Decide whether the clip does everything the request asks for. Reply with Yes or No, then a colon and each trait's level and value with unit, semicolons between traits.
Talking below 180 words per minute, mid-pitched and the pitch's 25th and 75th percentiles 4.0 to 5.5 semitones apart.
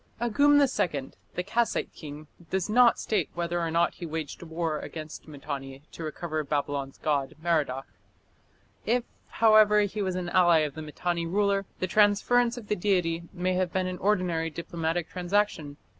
Yes: average, 160 wpm; medium, 175 Hz; average, 4.6 semitones